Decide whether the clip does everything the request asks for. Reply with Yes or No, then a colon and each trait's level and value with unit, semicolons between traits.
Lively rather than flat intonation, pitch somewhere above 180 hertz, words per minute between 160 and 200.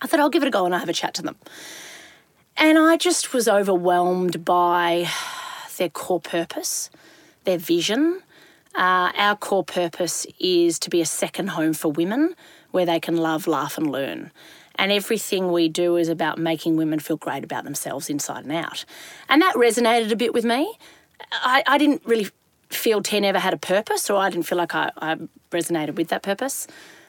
Yes: wide, 8.1 semitones; high, 190 Hz; average, 195 wpm